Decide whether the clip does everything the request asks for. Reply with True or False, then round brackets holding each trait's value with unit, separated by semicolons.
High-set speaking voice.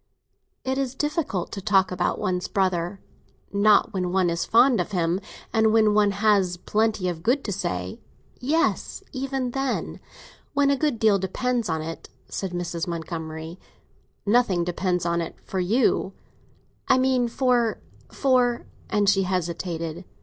True (195 Hz)